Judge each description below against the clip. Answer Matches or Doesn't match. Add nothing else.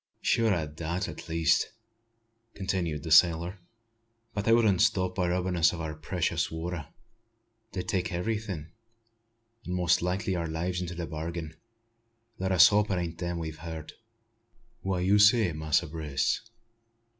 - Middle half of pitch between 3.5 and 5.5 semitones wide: Doesn't match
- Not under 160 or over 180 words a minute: Doesn't match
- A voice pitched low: Matches